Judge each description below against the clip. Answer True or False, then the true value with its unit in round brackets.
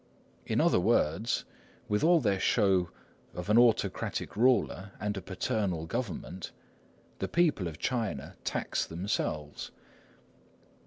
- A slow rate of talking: True (115 wpm)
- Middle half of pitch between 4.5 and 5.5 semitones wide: True (4.8 semitones)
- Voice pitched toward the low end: True (100 Hz)